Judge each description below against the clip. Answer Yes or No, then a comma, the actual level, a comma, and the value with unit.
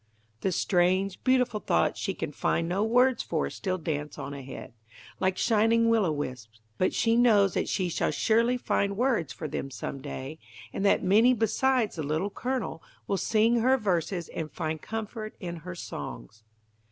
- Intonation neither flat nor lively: No, wide, 6.2 semitones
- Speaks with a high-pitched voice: Yes, high, 195 Hz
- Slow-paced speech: No, average, 175 wpm